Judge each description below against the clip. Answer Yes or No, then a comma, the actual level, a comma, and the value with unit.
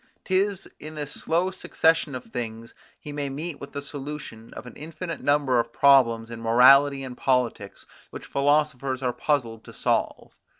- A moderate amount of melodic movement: Yes, average, 3.5 semitones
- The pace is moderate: Yes, average, 165 wpm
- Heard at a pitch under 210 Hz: Yes, medium, 140 Hz